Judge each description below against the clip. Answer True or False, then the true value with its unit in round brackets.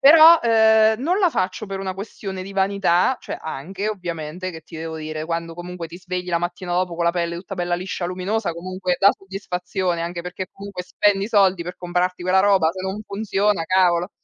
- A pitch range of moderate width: False (2.3 semitones)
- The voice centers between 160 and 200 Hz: True (185 Hz)